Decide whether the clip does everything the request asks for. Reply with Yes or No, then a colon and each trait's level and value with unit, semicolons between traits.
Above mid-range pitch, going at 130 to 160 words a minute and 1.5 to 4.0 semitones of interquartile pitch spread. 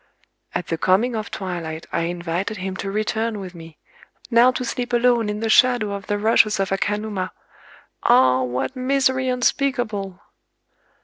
No: high, 210 Hz; average, 145 wpm; average, 4.7 semitones